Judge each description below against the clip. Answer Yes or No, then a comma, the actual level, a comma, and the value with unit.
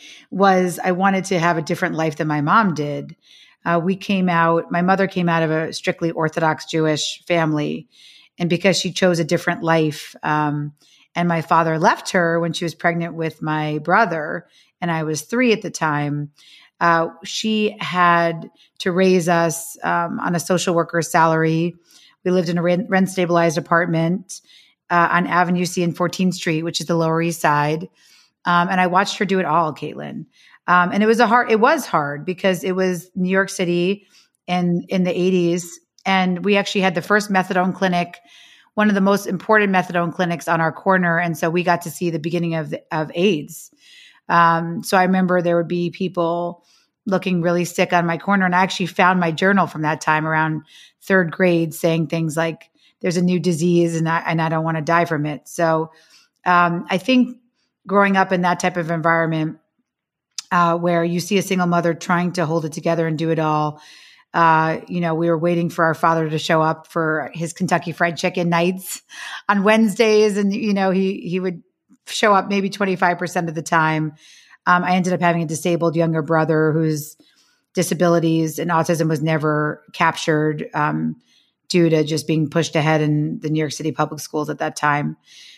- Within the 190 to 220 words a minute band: Yes, average, 195 wpm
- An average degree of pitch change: No, narrow, 2.3 semitones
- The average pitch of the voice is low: No, medium, 170 Hz